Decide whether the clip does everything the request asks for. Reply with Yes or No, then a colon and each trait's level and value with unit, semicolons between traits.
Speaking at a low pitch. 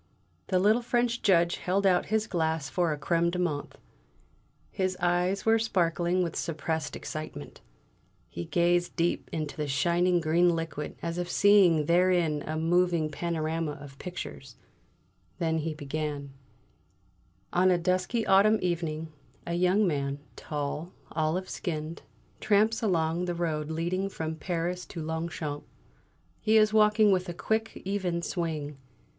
No: medium, 170 Hz